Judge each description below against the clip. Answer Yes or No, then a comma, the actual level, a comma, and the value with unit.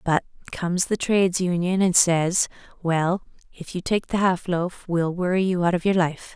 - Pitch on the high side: No, medium, 180 Hz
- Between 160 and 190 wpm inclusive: No, average, 200 wpm